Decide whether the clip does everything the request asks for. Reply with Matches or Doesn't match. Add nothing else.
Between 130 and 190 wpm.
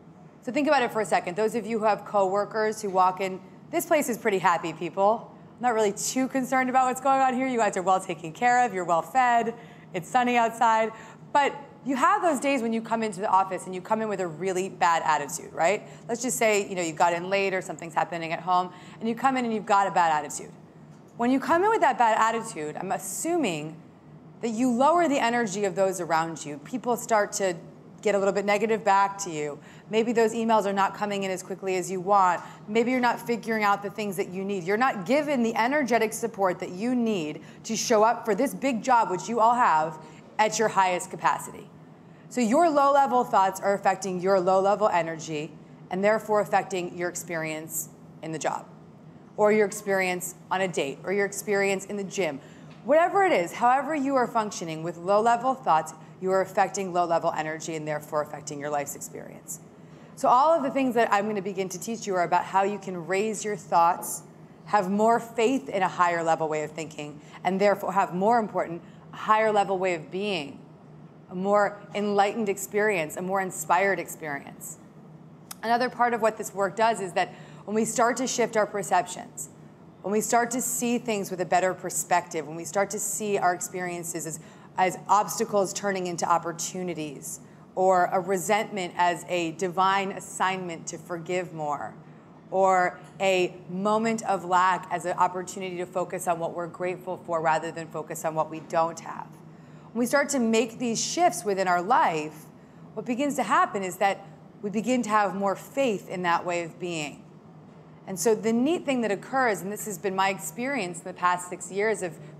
Doesn't match